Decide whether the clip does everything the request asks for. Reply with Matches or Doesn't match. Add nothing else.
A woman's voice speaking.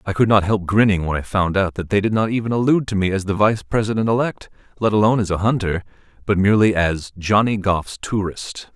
Doesn't match